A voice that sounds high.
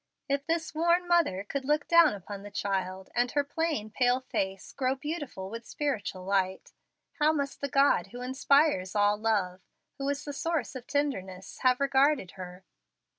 Yes: very high, 255 Hz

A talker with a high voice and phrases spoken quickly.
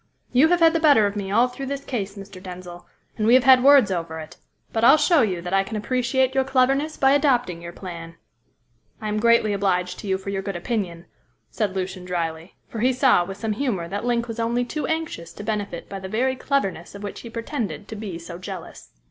Yes: high, 210 Hz; fast, 230 wpm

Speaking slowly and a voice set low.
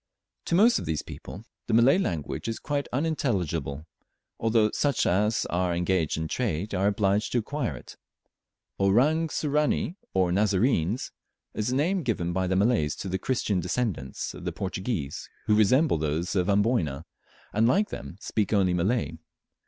No: average, 160 wpm; low, 105 Hz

